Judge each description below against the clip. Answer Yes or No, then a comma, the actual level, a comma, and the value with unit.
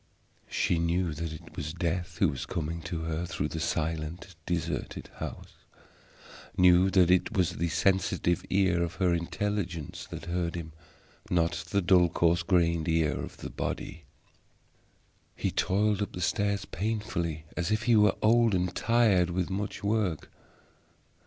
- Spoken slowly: No, average, 150 wpm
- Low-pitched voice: Yes, very low, 90 Hz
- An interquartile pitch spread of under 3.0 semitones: Yes, narrow, 2.6 semitones